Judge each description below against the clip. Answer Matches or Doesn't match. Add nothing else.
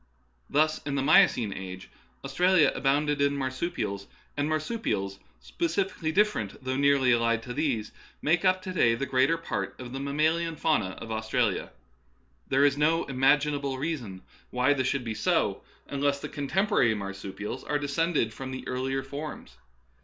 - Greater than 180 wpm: Doesn't match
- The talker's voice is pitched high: Doesn't match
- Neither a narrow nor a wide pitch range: Matches